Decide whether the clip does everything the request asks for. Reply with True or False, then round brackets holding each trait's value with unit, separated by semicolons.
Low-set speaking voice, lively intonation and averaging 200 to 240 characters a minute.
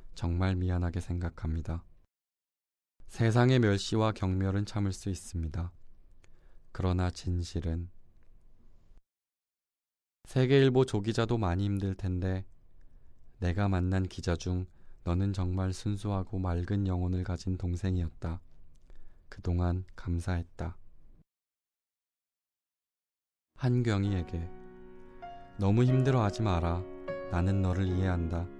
False (90 Hz; 2.4 semitones; 215 characters per minute)